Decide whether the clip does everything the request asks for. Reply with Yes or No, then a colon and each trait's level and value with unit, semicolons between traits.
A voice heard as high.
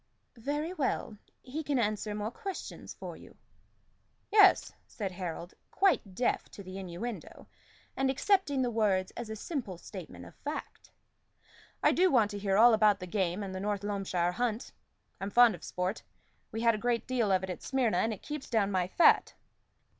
Yes: high, 215 Hz